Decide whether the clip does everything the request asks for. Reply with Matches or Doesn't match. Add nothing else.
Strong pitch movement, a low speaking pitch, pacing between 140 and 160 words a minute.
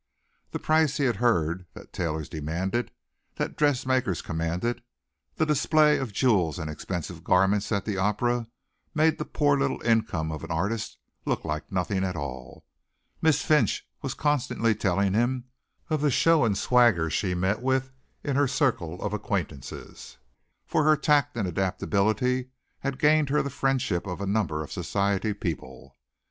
Matches